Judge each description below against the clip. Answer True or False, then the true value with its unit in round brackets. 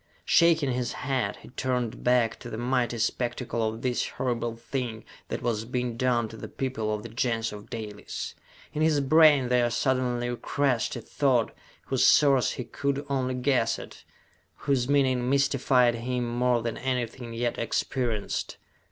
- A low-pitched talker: True (125 Hz)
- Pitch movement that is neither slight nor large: False (2.1 semitones)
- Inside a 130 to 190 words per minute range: True (160 wpm)